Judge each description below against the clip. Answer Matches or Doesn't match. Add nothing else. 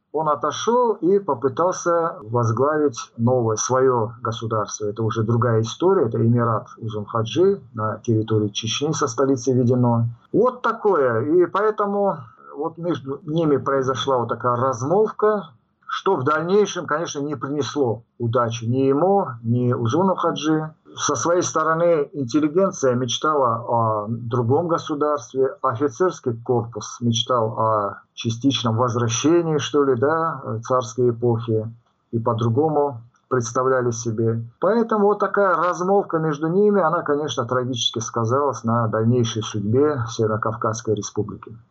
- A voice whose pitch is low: Matches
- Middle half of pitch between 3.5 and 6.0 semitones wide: Matches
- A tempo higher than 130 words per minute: Doesn't match